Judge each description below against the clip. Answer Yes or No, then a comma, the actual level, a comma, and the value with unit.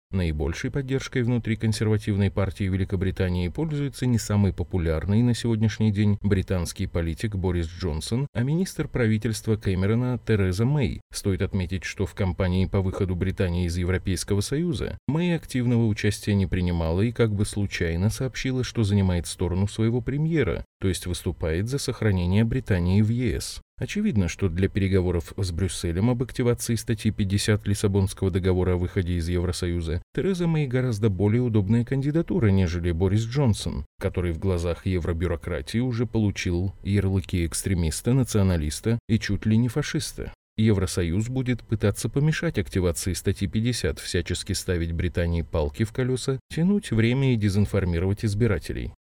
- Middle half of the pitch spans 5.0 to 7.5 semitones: No, average, 4.2 semitones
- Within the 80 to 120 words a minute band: No, average, 140 wpm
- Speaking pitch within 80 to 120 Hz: Yes, low, 100 Hz